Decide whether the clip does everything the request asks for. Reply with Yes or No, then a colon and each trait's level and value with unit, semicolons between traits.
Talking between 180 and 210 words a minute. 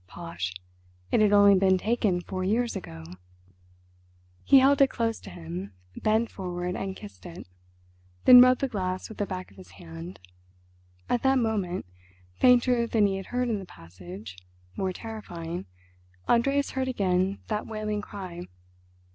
No: average, 155 wpm